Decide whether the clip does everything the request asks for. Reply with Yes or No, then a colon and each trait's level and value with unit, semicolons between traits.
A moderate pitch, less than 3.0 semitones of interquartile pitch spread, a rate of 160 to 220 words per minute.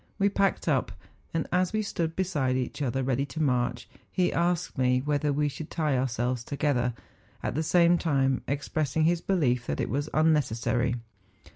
No: medium, 145 Hz; average, 4.5 semitones; average, 170 wpm